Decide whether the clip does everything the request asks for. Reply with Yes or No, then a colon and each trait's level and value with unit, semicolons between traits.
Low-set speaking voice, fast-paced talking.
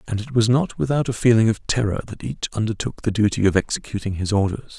Yes: low, 110 Hz; fast, 225 wpm